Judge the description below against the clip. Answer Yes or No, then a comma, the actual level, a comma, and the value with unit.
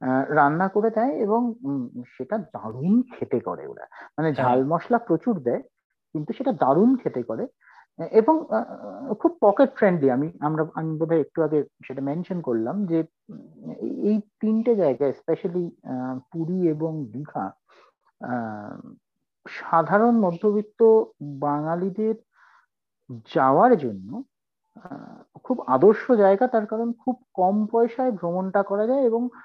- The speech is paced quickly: Yes, fast, 125 wpm